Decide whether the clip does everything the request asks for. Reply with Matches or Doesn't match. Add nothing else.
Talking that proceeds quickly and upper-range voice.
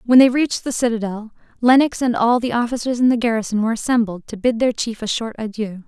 Matches